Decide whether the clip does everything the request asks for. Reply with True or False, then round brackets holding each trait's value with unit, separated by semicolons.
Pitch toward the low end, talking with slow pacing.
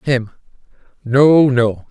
True (130 Hz; 95 wpm)